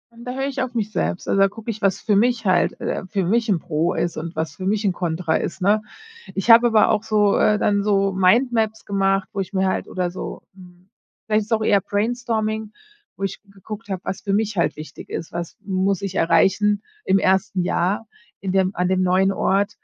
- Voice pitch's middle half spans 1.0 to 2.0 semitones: No, average, 2.7 semitones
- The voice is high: Yes, high, 195 Hz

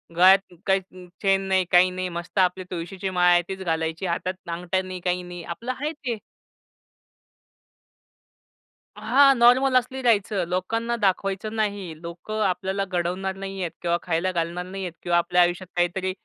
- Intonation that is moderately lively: No, narrow, 2.1 semitones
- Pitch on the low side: No, medium, 185 Hz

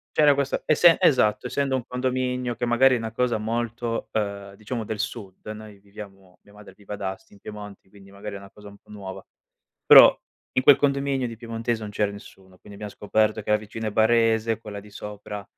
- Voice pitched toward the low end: Yes, low, 110 Hz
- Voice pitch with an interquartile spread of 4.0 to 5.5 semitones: No, average, 2.7 semitones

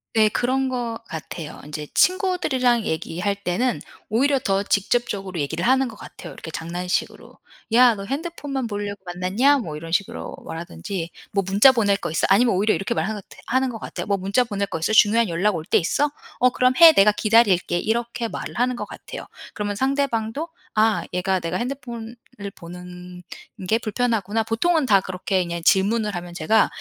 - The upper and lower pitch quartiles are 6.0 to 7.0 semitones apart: No, average, 5.1 semitones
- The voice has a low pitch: No, high, 210 Hz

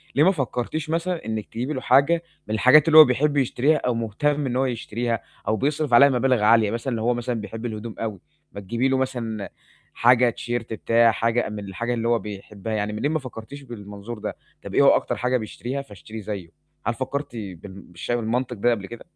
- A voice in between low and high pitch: No, low, 120 Hz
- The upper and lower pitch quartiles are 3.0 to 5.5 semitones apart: Yes, average, 3.4 semitones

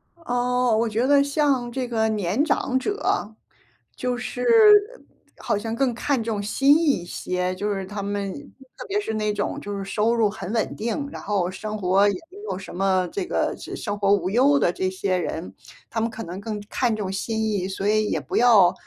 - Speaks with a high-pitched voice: Yes, high, 215 Hz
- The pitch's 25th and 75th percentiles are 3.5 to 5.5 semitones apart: Yes, average, 3.9 semitones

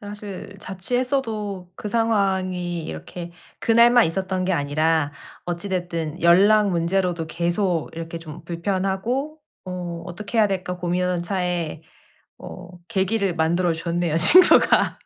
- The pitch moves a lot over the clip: No, average, 2.9 semitones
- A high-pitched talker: No, medium, 180 Hz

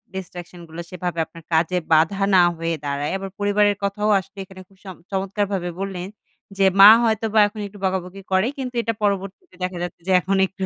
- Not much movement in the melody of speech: Yes, narrow, 2.3 semitones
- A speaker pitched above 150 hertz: Yes, high, 190 Hz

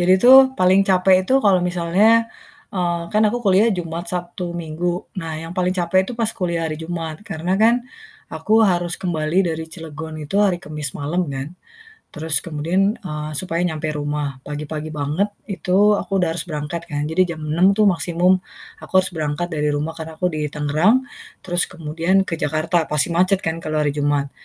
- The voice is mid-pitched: Yes, medium, 170 Hz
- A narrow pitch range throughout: No, average, 3.1 semitones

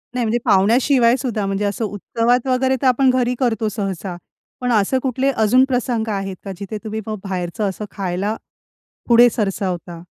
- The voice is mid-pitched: No, high, 220 Hz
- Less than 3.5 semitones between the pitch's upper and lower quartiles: No, average, 4.1 semitones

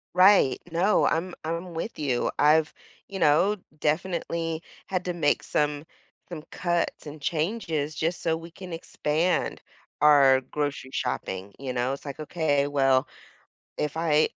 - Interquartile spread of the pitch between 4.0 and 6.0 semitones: No, average, 3.0 semitones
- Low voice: No, medium, 155 Hz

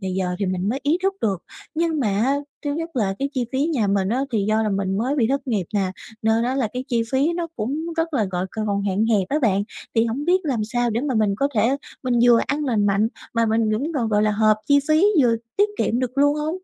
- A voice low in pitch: No, high, 230 Hz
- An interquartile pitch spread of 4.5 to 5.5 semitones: Yes, average, 5.2 semitones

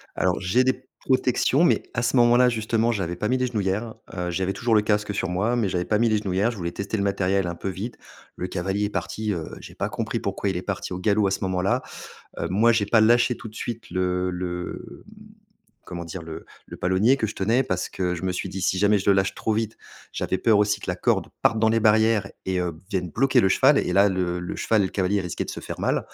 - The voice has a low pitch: Yes, low, 100 Hz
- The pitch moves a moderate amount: Yes, average, 3.4 semitones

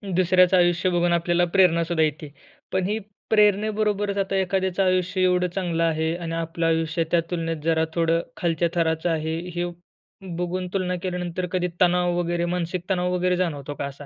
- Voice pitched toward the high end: No, medium, 175 Hz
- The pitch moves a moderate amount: No, narrow, 1.9 semitones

